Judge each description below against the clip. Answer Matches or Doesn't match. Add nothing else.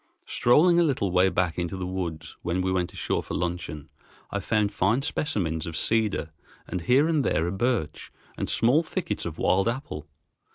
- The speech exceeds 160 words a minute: Matches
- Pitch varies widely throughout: Matches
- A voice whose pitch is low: Matches